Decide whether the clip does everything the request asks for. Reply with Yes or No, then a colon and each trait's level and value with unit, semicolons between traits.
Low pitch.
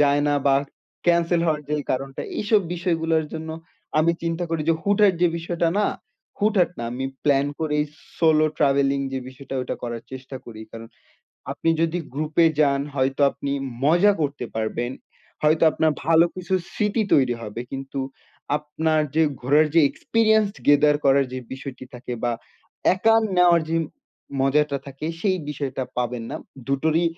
No: medium, 150 Hz